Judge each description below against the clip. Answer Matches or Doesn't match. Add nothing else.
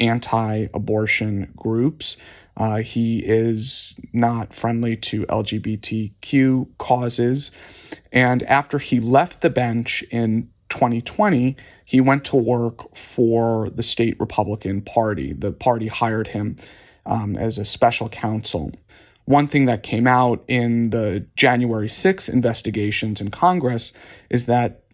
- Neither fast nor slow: Doesn't match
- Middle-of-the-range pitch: Doesn't match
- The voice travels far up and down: Doesn't match